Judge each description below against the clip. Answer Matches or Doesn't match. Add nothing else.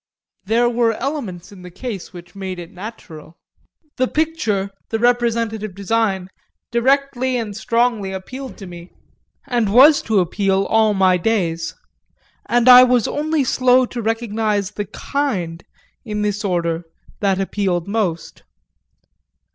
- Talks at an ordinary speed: Doesn't match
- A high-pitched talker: Matches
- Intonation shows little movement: Doesn't match